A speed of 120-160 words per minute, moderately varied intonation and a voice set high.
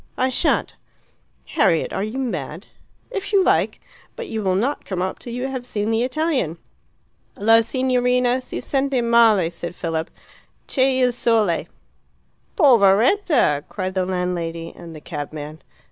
No: average, 145 wpm; wide, 6.4 semitones; high, 225 Hz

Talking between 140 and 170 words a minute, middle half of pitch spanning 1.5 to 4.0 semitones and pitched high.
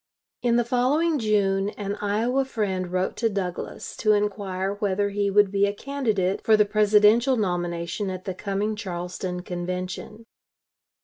Yes: average, 145 wpm; narrow, 2.6 semitones; high, 205 Hz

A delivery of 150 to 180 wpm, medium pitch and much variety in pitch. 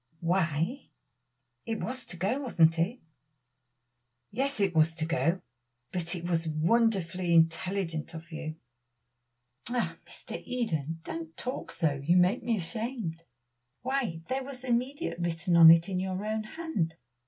No: average, 140 wpm; medium, 180 Hz; wide, 6.1 semitones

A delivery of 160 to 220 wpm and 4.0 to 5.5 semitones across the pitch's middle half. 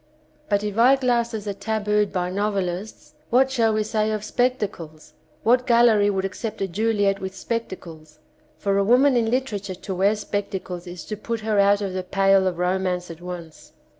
No: average, 180 wpm; average, 2.9 semitones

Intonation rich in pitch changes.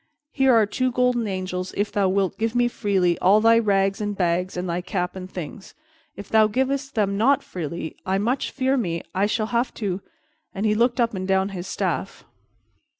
No: average, 3.8 semitones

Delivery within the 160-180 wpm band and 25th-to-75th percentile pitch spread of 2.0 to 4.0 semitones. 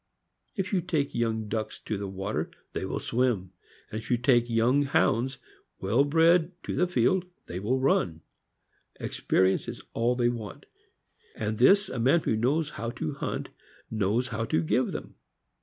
No: average, 170 wpm; average, 4.5 semitones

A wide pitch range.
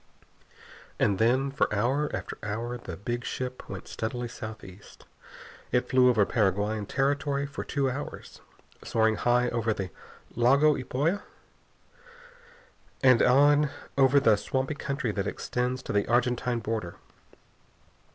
No: average, 3.6 semitones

